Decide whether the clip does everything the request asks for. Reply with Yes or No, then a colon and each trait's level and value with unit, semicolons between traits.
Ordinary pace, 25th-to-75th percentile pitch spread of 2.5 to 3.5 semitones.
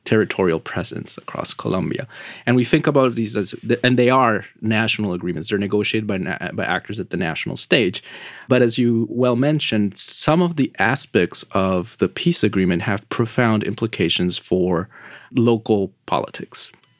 No: average, 160 wpm; average, 3.9 semitones